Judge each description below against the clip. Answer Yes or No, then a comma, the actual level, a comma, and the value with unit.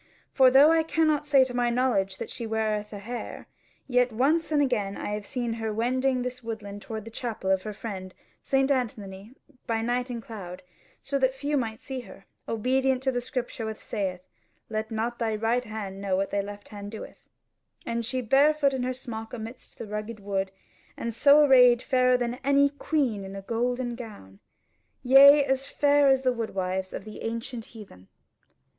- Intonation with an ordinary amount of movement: Yes, average, 3.7 semitones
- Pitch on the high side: Yes, high, 235 Hz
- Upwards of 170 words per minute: Yes, average, 190 wpm